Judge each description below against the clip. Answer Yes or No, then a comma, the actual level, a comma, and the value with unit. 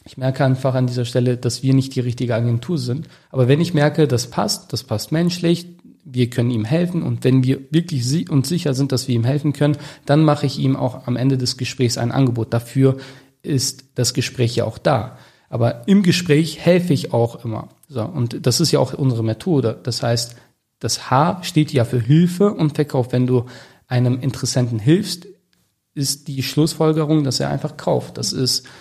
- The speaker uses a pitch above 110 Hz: Yes, low, 135 Hz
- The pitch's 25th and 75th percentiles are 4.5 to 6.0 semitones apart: No, average, 3.6 semitones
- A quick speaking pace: Yes, fast, 200 wpm